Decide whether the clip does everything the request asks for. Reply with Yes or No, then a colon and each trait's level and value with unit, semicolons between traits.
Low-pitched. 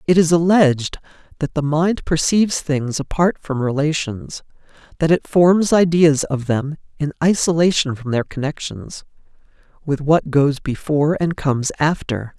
No: medium, 150 Hz